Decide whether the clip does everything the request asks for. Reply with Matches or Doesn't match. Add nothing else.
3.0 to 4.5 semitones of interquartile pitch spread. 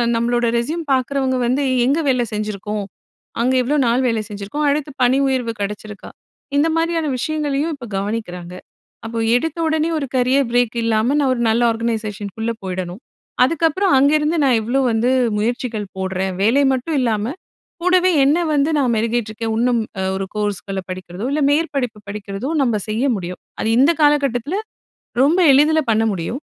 Doesn't match